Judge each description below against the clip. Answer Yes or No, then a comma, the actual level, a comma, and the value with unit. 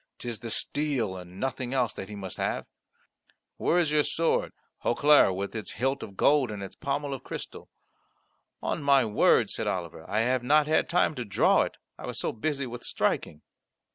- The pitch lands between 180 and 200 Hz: No, low, 125 Hz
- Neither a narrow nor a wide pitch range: No, wide, 5.7 semitones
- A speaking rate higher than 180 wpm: Yes, average, 190 wpm